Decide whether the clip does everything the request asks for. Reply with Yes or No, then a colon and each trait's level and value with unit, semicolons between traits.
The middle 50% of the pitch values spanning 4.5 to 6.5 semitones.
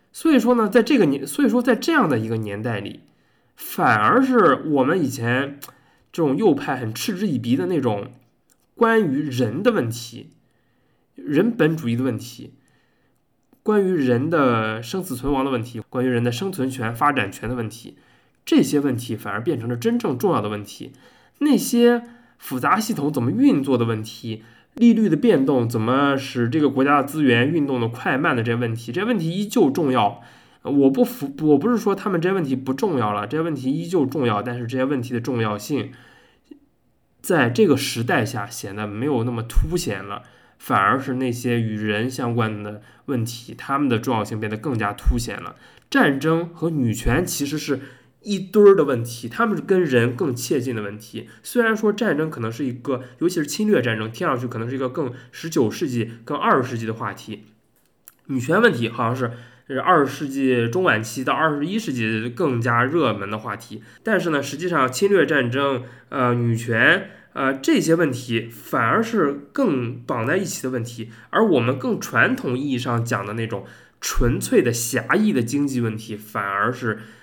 Yes: average, 5.3 semitones